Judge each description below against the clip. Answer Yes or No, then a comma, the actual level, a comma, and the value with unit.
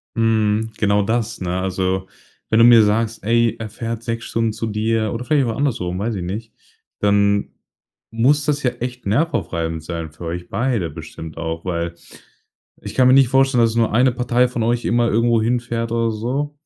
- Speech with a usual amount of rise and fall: Yes, average, 3.0 semitones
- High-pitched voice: No, low, 115 Hz